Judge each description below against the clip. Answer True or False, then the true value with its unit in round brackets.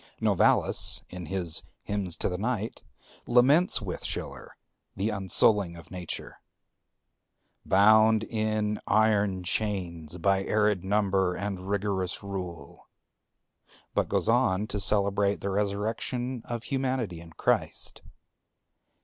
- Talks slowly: True (110 wpm)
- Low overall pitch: True (100 Hz)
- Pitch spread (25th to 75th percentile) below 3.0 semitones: True (2.5 semitones)